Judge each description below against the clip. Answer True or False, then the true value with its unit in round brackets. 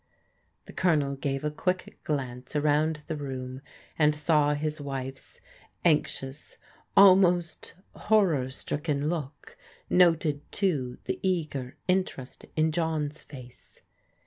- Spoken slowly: True (110 wpm)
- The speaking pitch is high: False (150 Hz)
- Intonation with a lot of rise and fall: False (3.4 semitones)